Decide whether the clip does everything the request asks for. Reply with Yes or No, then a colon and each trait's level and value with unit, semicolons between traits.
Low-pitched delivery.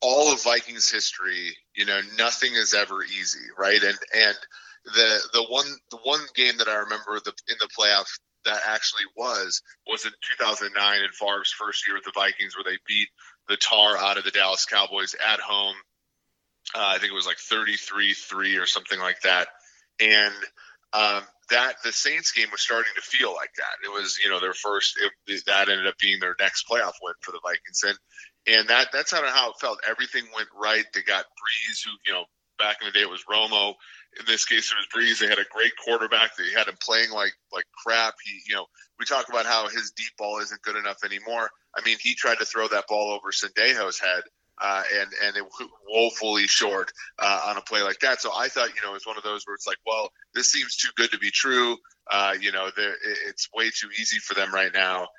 Yes: low, 110 Hz